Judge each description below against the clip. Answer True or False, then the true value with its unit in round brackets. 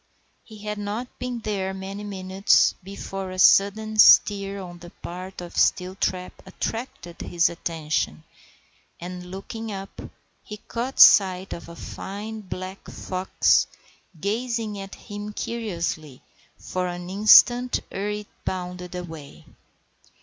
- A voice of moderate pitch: False (195 Hz)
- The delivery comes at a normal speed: False (120 wpm)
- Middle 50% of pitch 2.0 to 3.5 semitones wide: True (2.7 semitones)